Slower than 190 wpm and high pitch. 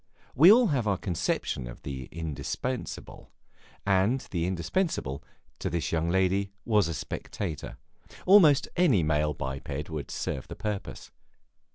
No: slow, 135 wpm; very low, 90 Hz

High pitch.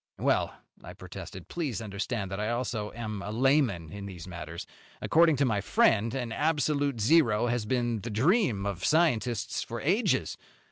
No: low, 115 Hz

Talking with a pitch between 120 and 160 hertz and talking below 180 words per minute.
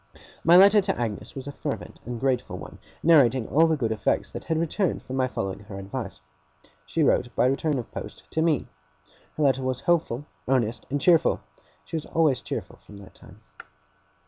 No: low, 135 Hz; average, 190 wpm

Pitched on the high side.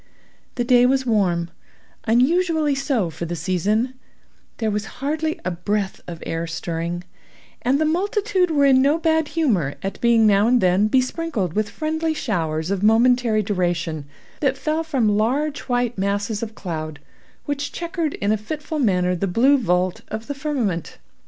Yes: high, 225 Hz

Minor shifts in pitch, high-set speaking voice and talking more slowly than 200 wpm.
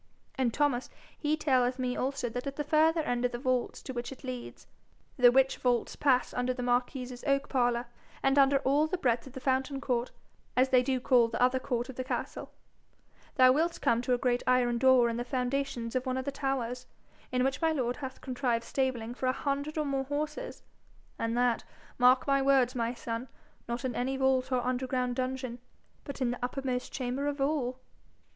No: narrow, 1.8 semitones; very high, 255 Hz; fast, 205 wpm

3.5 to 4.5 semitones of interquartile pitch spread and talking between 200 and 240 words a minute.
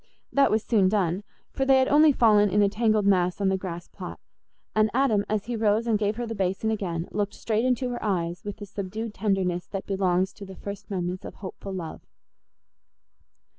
No: average, 2.7 semitones; fast, 205 wpm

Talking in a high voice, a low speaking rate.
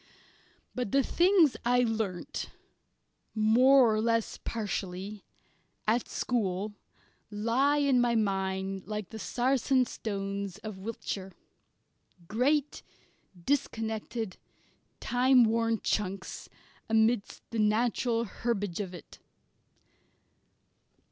Yes: high, 220 Hz; slow, 90 wpm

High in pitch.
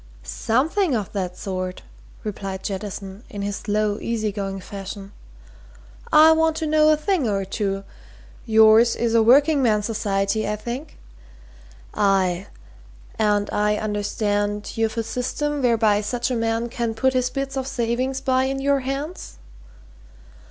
Yes: high, 225 Hz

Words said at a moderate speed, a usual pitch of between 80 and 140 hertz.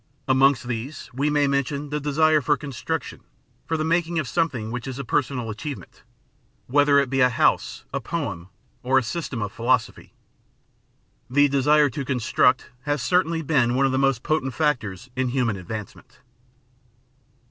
Yes: average, 160 wpm; low, 135 Hz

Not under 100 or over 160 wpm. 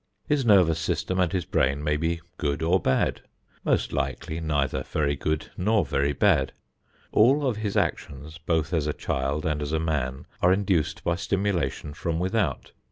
No: average, 170 wpm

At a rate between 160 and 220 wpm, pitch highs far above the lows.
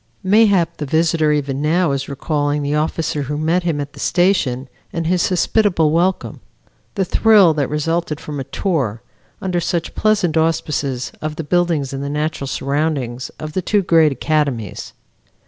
No: average, 165 wpm; average, 3.4 semitones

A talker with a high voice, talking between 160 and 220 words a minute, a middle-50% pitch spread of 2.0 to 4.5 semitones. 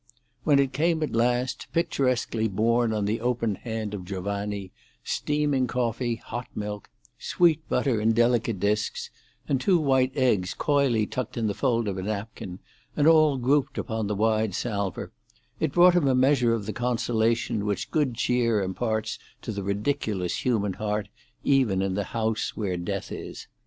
No: low, 115 Hz; average, 165 wpm; average, 3.9 semitones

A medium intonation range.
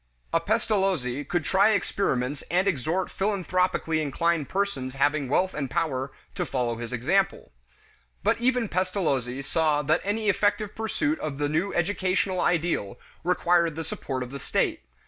No: wide, 5.9 semitones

